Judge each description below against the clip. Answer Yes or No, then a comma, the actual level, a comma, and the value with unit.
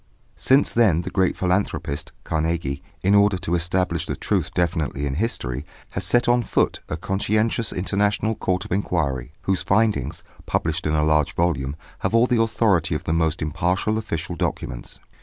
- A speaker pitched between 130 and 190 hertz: No, very low, 90 Hz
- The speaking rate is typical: Yes, average, 165 wpm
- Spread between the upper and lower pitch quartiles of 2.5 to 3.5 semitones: No, average, 4.8 semitones